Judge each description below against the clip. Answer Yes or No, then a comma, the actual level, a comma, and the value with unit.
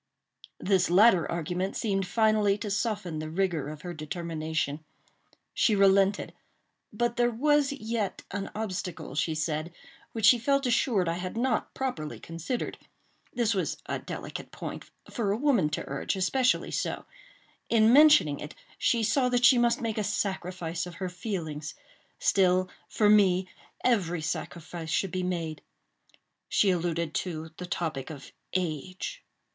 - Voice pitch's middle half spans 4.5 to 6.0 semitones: Yes, average, 5.0 semitones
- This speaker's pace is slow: No, average, 145 wpm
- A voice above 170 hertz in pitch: Yes, medium, 185 Hz